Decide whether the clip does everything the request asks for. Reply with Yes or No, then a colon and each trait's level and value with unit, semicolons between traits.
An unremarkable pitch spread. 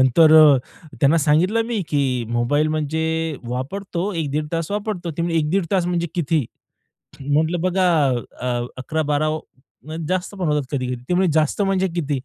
Yes: average, 3.5 semitones